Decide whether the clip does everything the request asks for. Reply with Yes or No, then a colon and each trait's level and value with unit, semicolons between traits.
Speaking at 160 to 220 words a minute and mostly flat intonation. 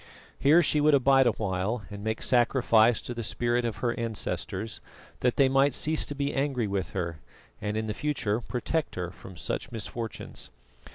No: average, 170 wpm; average, 4.3 semitones